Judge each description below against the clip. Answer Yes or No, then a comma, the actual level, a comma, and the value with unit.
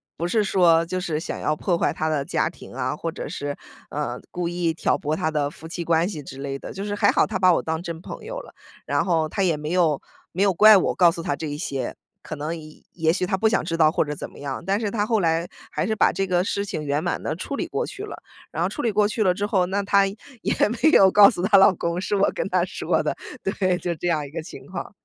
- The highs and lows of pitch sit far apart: No, average, 3.8 semitones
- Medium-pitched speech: Yes, medium, 175 Hz